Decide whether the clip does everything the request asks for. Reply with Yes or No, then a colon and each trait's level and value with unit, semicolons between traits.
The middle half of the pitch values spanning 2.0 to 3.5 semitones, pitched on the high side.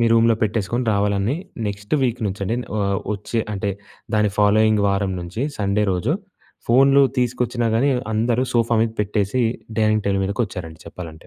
No: average, 2.8 semitones; low, 105 Hz